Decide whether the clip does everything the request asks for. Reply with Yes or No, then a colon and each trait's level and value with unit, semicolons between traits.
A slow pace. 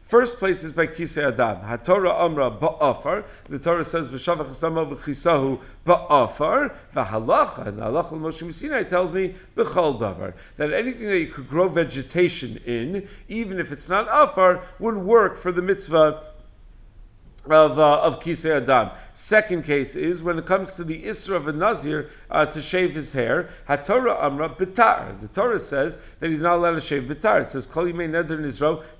No: average, 170 wpm